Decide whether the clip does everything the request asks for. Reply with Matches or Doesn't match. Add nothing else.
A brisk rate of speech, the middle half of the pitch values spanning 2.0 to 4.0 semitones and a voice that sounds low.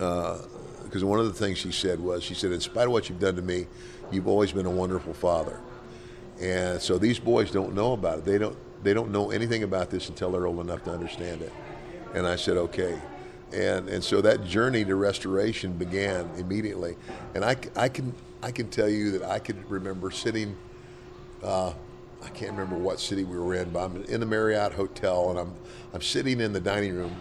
Matches